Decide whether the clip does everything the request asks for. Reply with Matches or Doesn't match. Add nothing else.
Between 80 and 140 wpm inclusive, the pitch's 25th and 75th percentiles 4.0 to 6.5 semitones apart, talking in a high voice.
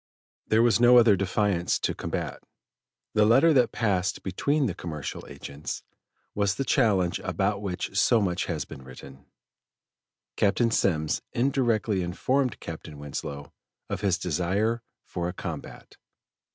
Doesn't match